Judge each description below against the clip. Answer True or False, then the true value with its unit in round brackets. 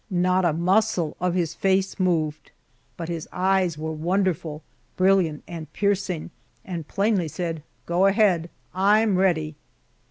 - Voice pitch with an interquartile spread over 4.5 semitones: False (2.9 semitones)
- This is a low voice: False (180 Hz)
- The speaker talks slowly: True (130 wpm)